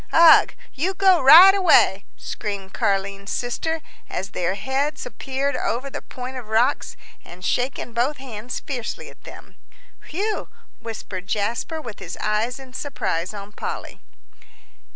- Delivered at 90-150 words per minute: Yes, slow, 135 wpm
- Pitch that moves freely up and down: Yes, wide, 5.8 semitones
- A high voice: Yes, high, 245 Hz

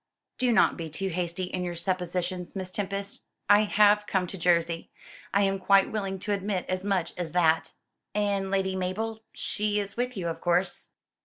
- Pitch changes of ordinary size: No, narrow, 2.3 semitones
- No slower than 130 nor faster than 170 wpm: No, average, 180 wpm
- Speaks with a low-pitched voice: No, high, 190 Hz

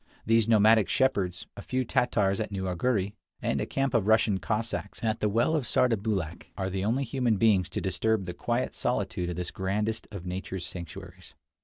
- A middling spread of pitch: Yes, average, 3.3 semitones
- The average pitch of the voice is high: No, low, 105 Hz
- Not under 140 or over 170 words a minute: No, average, 185 wpm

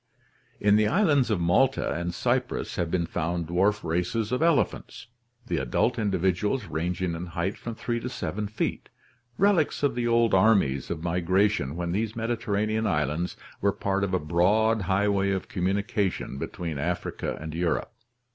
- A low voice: Yes, low, 100 Hz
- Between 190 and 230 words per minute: No, average, 160 wpm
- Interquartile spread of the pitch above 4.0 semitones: Yes, average, 4.5 semitones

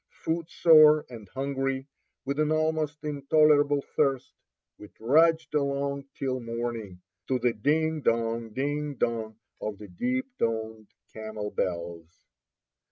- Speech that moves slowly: Yes, slow, 115 wpm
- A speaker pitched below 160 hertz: Yes, low, 135 Hz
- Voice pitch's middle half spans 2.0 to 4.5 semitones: No, average, 5.3 semitones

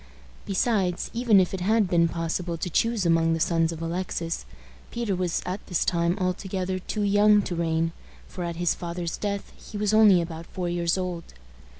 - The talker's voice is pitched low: No, medium, 180 Hz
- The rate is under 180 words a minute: No, average, 185 wpm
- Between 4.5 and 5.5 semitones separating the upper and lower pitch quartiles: No, average, 2.9 semitones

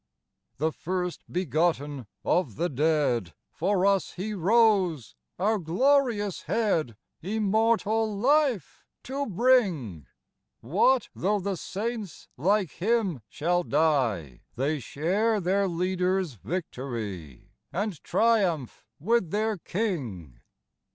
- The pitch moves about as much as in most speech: No, wide, 6.3 semitones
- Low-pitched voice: No, medium, 180 Hz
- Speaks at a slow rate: Yes, slow, 100 wpm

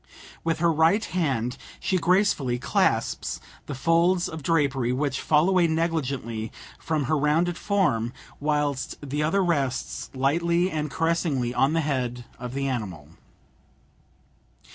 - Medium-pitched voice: Yes, medium, 150 Hz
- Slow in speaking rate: Yes, slow, 130 wpm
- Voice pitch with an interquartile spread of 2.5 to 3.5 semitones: No, average, 4.3 semitones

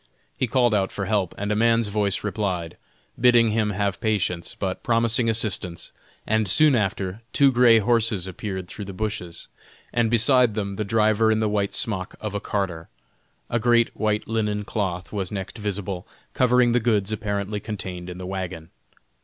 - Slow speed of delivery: No, average, 170 wpm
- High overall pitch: No, low, 105 Hz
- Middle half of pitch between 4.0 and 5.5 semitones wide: No, average, 2.9 semitones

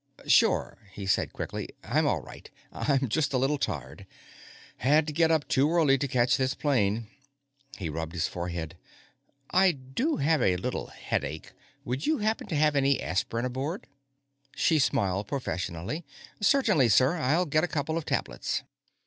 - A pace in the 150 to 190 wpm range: Yes, average, 160 wpm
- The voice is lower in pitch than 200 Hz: Yes, low, 135 Hz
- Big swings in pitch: Yes, wide, 7.3 semitones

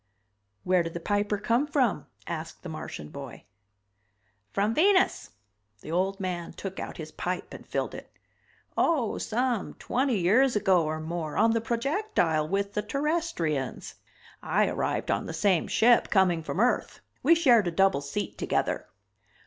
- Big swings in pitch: Yes, wide, 6.2 semitones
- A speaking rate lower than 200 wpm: Yes, average, 155 wpm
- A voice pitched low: No, high, 200 Hz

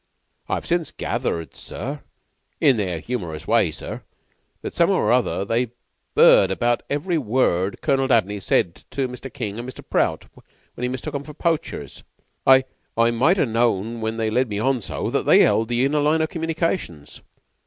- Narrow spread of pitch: No, average, 5.1 semitones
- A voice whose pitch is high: No, low, 120 Hz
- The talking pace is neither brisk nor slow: Yes, average, 175 wpm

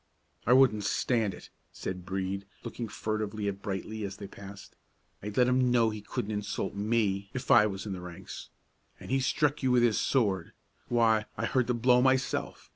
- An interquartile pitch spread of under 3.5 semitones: No, average, 3.9 semitones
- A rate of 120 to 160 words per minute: No, average, 190 wpm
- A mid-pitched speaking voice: No, low, 110 Hz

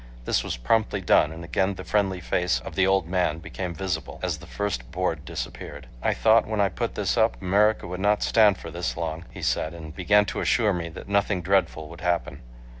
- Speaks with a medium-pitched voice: No, very low, 90 Hz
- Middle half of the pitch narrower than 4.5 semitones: Yes, average, 3.3 semitones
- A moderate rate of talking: No, fast, 215 wpm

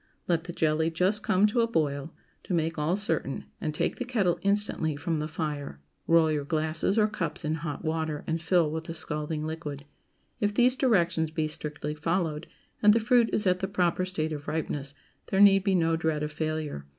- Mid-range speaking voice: Yes, medium, 160 Hz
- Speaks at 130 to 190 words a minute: No, average, 200 wpm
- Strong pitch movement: No, average, 3.6 semitones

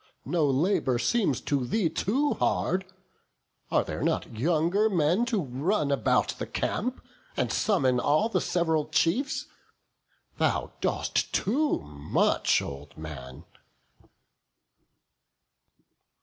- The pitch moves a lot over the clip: Yes, wide, 8.4 semitones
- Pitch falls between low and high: Yes, medium, 160 Hz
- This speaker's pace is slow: Yes, slow, 105 wpm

